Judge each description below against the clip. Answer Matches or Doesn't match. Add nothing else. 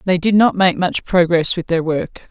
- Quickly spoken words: Matches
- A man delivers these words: Doesn't match